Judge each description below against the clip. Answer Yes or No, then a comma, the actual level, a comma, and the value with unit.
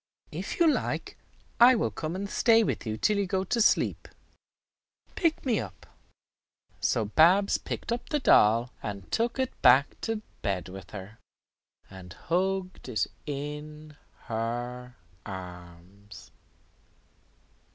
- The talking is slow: Yes, slow, 130 wpm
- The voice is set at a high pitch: No, medium, 140 Hz